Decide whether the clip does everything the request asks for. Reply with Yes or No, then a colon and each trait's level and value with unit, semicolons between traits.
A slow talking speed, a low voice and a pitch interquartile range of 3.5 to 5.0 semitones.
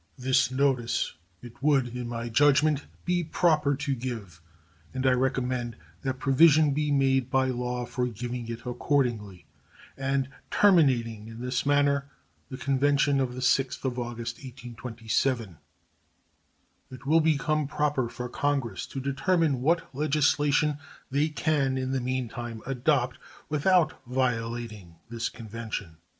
No: slow, 130 wpm; low, 130 Hz; average, 3.0 semitones